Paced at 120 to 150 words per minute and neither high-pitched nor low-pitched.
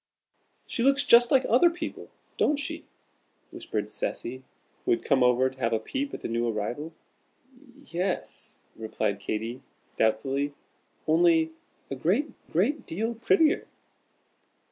Yes: average, 140 wpm; medium, 160 Hz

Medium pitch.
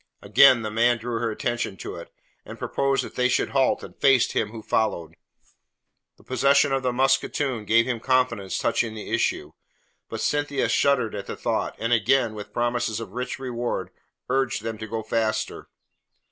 No: low, 120 Hz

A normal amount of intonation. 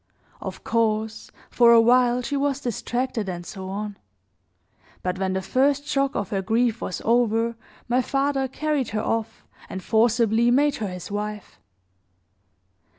Yes: average, 3.5 semitones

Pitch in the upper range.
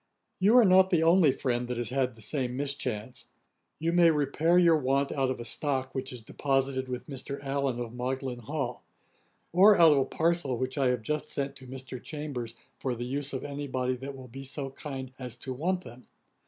No: low, 135 Hz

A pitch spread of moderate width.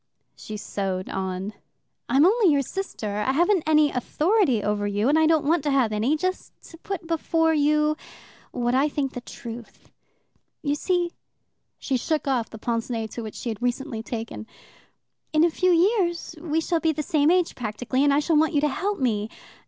No: wide, 6.0 semitones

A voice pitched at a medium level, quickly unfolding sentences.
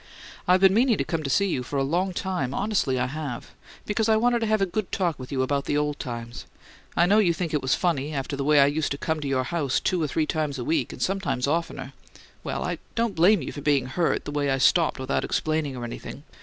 Yes: medium, 150 Hz; fast, 255 wpm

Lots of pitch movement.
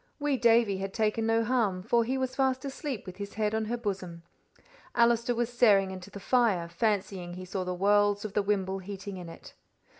No: average, 3.8 semitones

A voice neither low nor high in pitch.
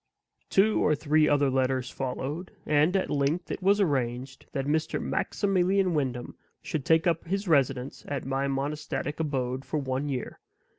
Yes: medium, 145 Hz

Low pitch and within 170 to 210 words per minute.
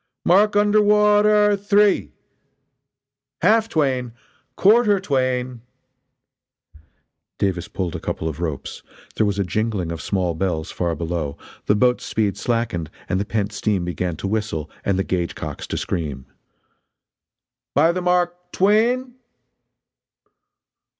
No: low, 115 Hz; slow, 135 wpm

